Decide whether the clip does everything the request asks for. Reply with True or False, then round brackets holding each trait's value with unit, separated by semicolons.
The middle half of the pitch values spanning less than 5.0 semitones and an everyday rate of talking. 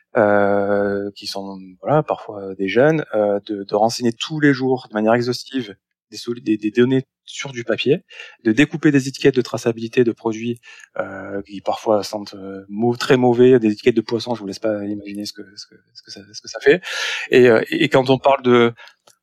True (3.6 semitones; 210 wpm)